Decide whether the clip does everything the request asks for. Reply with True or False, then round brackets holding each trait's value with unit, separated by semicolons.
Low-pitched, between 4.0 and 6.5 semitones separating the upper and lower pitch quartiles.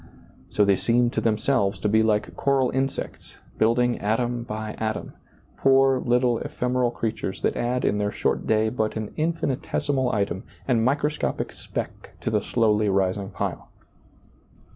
False (115 Hz; 2.9 semitones)